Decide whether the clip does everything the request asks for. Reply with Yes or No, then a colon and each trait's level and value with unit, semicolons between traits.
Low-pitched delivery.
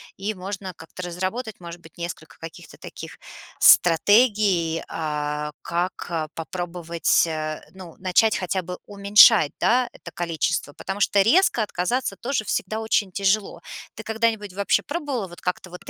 No: medium, 185 Hz